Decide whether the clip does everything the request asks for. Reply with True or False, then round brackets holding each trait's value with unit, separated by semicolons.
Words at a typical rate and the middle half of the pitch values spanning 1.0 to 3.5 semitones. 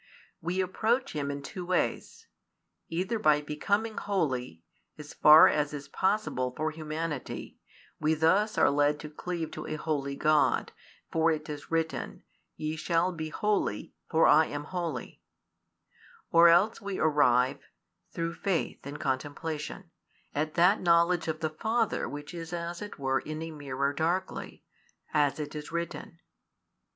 True (145 wpm; 2.9 semitones)